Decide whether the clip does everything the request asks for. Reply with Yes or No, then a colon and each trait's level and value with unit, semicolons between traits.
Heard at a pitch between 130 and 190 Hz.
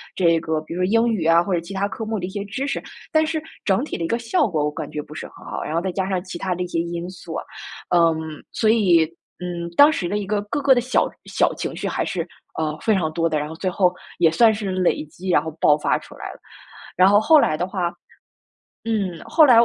Yes: medium, 185 Hz